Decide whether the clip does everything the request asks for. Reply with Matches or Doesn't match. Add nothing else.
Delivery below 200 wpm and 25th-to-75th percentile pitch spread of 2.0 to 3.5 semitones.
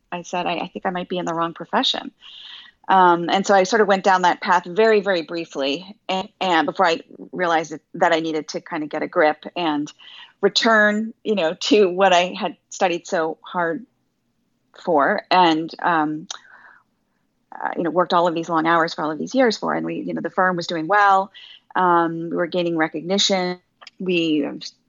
Doesn't match